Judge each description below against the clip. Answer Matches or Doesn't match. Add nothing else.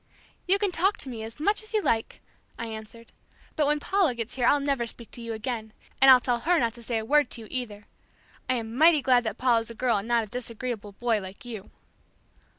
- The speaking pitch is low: Doesn't match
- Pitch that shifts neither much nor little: Matches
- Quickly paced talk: Matches